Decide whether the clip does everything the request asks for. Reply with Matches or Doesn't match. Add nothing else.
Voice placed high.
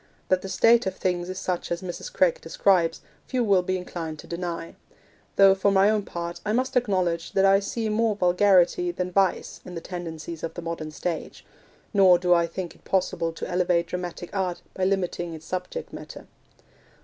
Doesn't match